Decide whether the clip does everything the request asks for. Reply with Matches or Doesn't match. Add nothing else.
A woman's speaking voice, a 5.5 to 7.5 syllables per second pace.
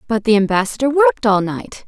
Matches